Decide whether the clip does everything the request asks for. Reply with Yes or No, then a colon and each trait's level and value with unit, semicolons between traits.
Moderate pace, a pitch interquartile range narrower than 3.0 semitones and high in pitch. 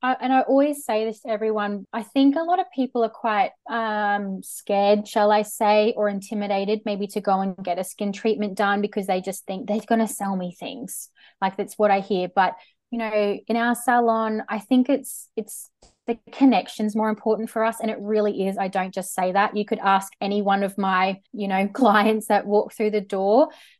No: fast, 220 wpm; narrow, 2.4 semitones; high, 210 Hz